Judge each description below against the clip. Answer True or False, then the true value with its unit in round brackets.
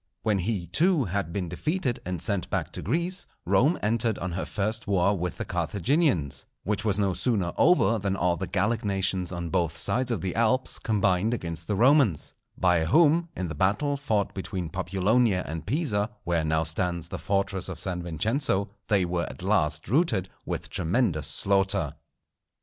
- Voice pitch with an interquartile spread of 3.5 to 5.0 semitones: True (4.5 semitones)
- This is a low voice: True (100 Hz)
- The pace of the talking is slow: False (175 wpm)